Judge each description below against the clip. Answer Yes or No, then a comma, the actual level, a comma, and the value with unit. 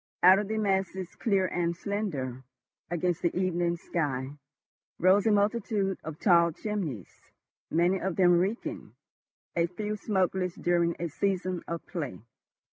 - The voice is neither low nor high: Yes, medium, 180 Hz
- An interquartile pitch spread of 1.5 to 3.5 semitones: Yes, narrow, 2.6 semitones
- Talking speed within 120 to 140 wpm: Yes, slow, 135 wpm